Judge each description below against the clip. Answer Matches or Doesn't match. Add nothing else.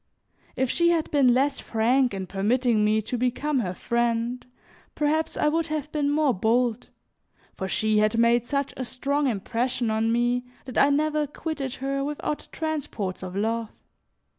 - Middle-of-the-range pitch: Doesn't match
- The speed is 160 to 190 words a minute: Matches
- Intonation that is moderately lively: Matches